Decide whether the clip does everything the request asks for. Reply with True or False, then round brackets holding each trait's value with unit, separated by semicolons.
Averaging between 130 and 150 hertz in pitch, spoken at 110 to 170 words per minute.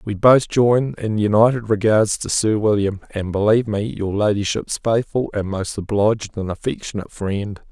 False (105 Hz; 165 wpm)